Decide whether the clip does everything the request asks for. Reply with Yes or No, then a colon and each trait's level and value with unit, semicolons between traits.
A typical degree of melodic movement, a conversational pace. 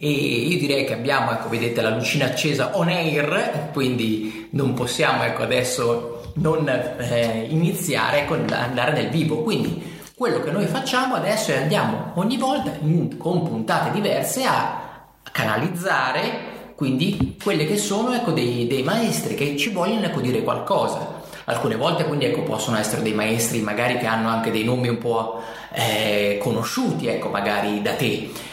No: wide, 6.7 semitones; average, 160 wpm